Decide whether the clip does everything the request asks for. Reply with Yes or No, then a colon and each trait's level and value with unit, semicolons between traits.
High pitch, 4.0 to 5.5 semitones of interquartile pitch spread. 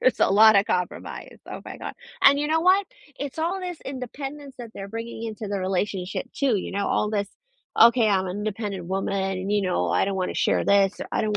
Yes: high, 210 Hz; average, 4.9 semitones